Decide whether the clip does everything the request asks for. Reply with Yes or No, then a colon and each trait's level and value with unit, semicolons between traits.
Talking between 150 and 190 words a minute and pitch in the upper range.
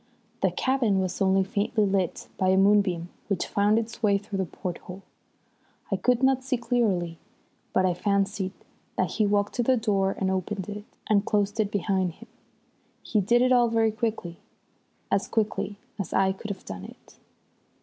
Yes: average, 175 wpm; high, 200 Hz